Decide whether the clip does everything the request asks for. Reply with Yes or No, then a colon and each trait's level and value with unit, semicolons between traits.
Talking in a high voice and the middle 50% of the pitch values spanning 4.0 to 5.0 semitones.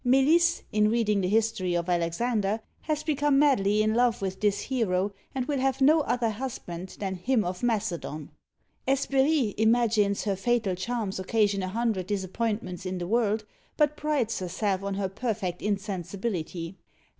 Yes: high, 215 Hz; average, 4.5 semitones